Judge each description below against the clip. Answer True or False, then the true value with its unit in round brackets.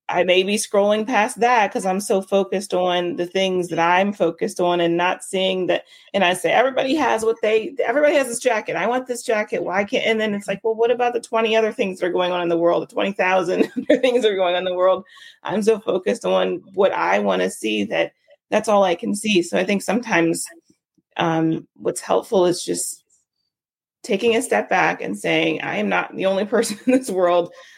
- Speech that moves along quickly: True (225 wpm)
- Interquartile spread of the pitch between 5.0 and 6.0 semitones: False (4.2 semitones)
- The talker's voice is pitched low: False (190 Hz)